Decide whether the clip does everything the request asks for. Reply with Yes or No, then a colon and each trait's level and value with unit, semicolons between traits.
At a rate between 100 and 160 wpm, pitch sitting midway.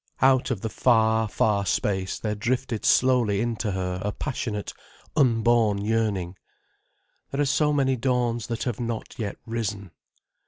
No: average, 150 wpm; low, 115 Hz